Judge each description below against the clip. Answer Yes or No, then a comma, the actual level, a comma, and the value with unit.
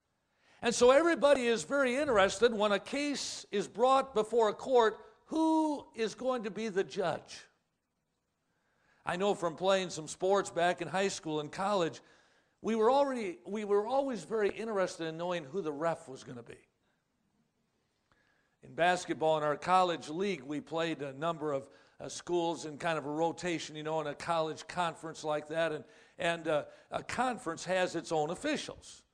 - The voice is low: No, medium, 180 Hz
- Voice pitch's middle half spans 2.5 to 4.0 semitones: No, wide, 5.6 semitones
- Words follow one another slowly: No, average, 175 wpm